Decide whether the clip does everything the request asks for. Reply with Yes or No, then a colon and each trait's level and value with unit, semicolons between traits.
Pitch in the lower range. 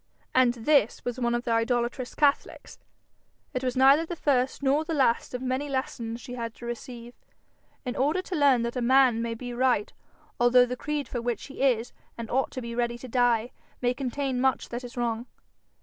No: very high, 250 Hz